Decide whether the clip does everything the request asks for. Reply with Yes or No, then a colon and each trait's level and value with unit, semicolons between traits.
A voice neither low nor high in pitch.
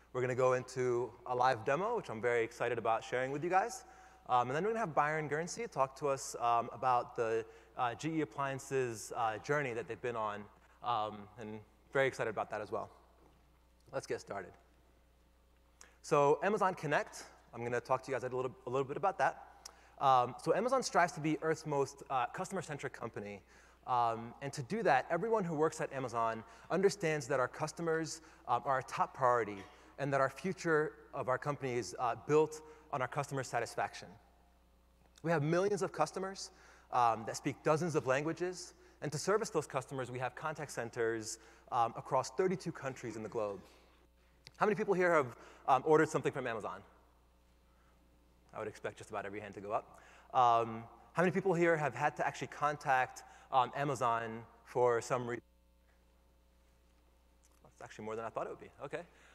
No: low, 130 Hz